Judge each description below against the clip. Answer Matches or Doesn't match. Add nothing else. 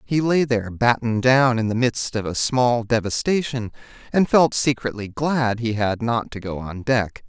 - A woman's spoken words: Doesn't match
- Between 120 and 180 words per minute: Doesn't match